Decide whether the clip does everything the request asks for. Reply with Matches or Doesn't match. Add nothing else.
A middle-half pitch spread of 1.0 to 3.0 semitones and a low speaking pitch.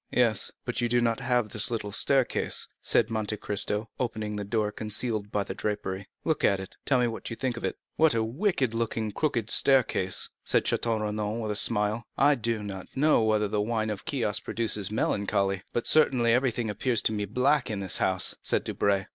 Matches